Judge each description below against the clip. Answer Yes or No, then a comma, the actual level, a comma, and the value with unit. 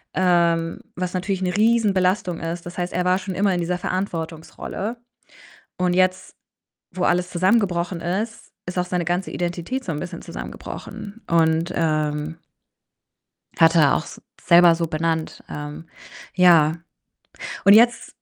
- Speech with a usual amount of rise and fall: No, narrow, 2.0 semitones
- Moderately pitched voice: Yes, medium, 175 Hz